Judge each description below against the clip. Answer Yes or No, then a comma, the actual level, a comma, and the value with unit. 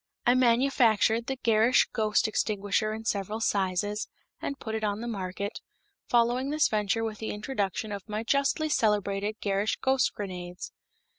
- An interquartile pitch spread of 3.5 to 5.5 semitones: No, narrow, 2.6 semitones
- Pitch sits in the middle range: No, high, 215 Hz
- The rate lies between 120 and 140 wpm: No, average, 150 wpm